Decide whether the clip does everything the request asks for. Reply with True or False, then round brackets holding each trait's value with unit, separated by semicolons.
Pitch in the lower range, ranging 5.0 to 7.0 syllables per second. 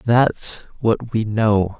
False (110 Hz; 2.7 syllables/s)